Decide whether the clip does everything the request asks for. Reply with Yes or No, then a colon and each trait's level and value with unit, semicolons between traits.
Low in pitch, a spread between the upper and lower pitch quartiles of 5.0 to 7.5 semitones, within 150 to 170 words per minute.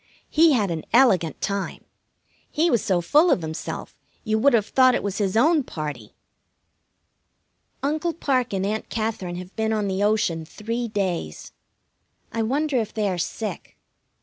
No: high, 215 Hz; wide, 5.4 semitones; average, 160 wpm